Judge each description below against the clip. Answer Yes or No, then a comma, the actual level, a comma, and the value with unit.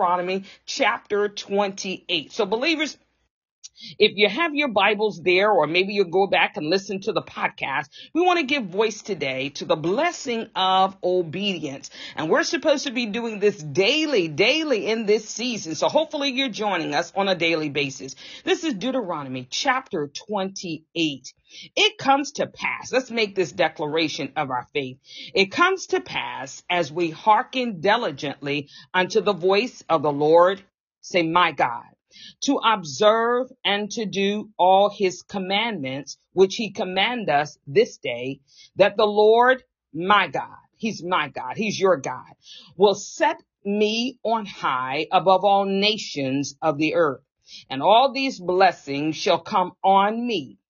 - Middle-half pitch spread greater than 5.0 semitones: Yes, wide, 5.5 semitones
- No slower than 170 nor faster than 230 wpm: No, average, 155 wpm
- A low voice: No, high, 195 Hz